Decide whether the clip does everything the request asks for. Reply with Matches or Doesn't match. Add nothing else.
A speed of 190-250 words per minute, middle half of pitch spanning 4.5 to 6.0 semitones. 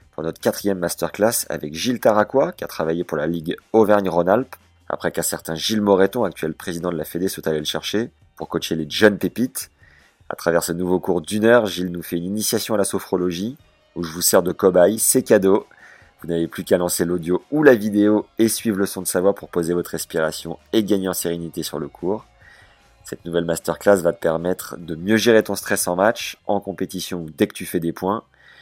Doesn't match